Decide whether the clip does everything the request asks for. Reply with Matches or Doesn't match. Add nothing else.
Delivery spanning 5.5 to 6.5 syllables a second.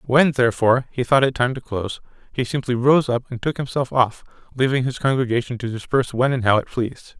Matches